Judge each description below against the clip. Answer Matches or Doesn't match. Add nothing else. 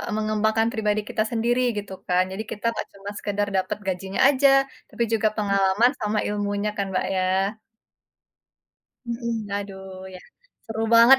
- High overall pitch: Matches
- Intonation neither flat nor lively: Doesn't match